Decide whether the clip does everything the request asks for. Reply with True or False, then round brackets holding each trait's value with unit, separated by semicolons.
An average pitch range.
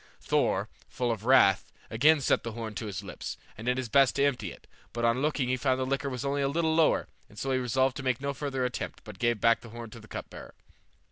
True (3.0 semitones)